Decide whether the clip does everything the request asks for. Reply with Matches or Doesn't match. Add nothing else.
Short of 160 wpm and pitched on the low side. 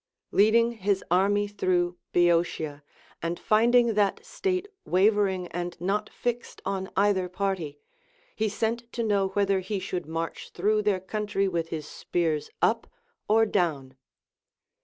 Doesn't match